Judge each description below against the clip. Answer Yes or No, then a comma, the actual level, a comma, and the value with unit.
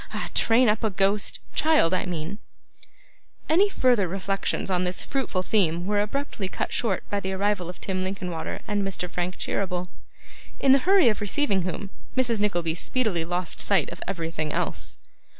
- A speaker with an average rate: Yes, average, 170 wpm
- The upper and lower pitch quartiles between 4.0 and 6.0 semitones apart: No, average, 3.3 semitones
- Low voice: No, high, 195 Hz